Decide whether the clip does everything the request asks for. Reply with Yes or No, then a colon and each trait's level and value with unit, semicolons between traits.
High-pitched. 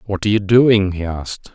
No: low, 100 Hz